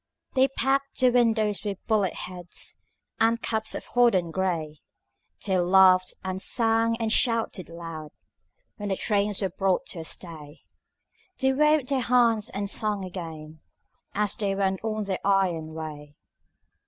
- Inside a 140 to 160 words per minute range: Yes, average, 145 wpm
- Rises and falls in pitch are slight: No, average, 4.3 semitones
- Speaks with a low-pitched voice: No, high, 200 Hz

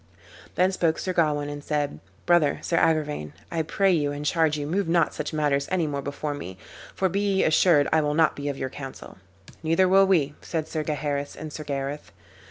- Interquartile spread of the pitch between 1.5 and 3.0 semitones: Yes, narrow, 2.6 semitones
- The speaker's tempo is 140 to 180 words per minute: No, fast, 205 wpm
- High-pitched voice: No, medium, 150 Hz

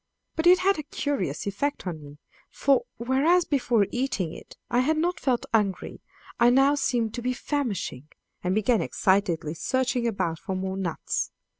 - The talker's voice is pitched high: Yes, high, 240 Hz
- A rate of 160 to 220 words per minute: Yes, average, 165 wpm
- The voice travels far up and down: Yes, wide, 6.6 semitones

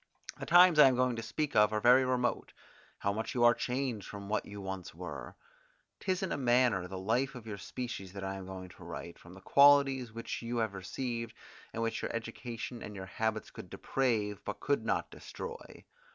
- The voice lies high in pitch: No, low, 115 Hz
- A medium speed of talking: No, fast, 210 wpm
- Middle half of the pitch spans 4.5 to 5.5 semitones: No, average, 4.1 semitones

